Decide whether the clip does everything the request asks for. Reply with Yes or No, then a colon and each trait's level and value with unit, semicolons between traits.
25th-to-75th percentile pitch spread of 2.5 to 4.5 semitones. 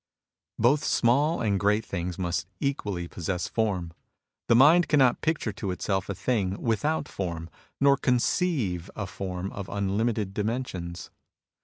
No: wide, 5.4 semitones